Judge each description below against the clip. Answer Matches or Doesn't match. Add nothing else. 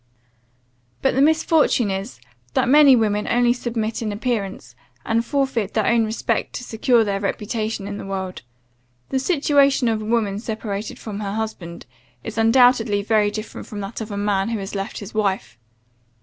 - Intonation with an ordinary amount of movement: Matches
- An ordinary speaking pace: Matches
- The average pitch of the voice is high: Matches